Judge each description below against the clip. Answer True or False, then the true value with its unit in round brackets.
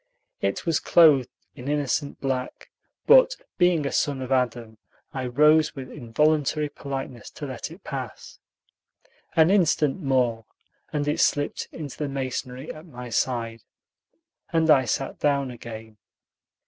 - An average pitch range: True (3.4 semitones)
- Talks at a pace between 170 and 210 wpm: False (135 wpm)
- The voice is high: False (135 Hz)